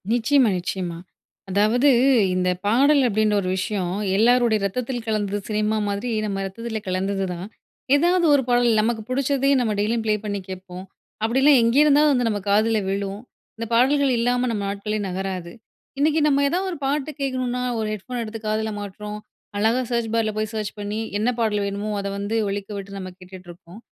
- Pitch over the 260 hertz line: No, high, 215 Hz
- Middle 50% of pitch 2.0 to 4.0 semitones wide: Yes, average, 3.7 semitones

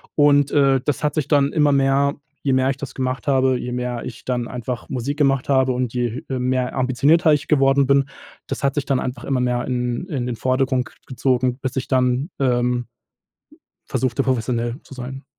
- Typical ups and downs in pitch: No, narrow, 1.9 semitones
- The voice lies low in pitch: Yes, low, 130 Hz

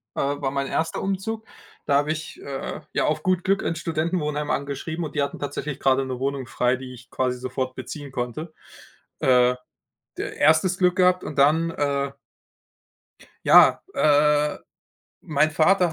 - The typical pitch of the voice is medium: Yes, medium, 150 Hz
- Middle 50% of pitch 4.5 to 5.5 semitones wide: No, average, 3.2 semitones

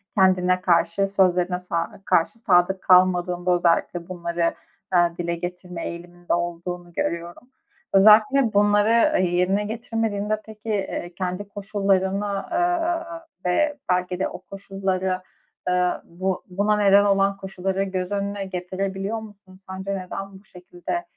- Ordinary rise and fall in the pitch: No, narrow, 2.2 semitones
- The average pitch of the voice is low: No, high, 190 Hz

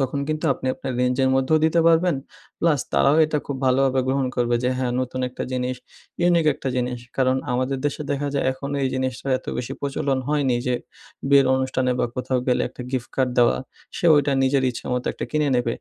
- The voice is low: Yes, low, 130 Hz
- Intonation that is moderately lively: No, narrow, 2.0 semitones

